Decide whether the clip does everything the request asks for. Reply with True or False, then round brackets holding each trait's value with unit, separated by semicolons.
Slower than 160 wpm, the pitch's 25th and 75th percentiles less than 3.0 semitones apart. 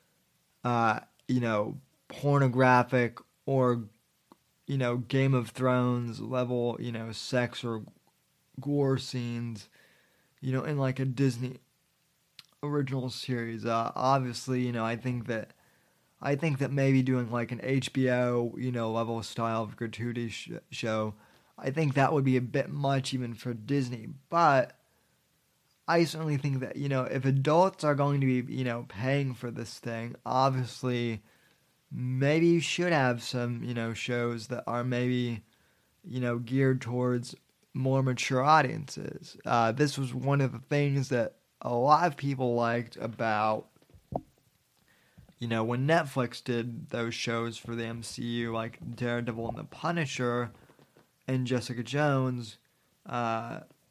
True (145 wpm; 2.5 semitones)